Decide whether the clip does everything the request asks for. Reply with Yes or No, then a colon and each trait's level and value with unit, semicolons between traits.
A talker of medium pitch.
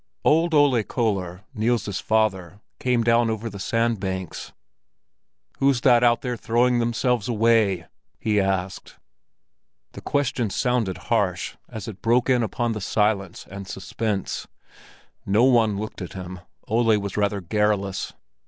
No: low, 110 Hz